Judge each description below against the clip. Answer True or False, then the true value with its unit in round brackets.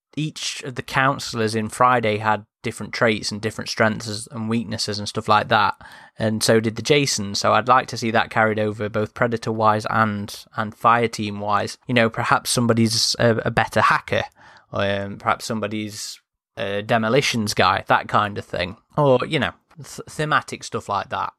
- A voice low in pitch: True (110 Hz)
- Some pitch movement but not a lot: False (1.8 semitones)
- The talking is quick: False (185 wpm)